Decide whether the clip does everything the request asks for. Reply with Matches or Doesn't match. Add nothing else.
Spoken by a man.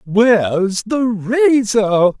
Matches